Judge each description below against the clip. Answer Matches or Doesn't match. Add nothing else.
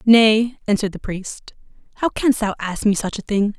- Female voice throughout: Matches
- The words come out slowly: Doesn't match